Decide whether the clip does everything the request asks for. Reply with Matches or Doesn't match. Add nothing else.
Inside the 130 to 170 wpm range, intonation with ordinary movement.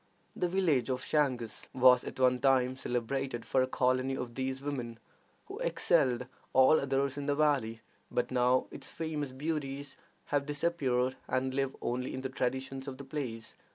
Doesn't match